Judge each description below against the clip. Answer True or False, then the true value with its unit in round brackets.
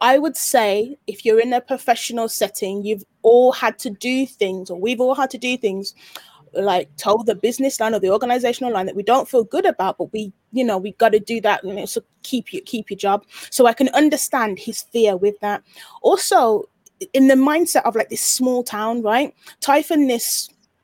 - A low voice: False (235 Hz)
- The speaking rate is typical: False (215 wpm)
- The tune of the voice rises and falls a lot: False (4.2 semitones)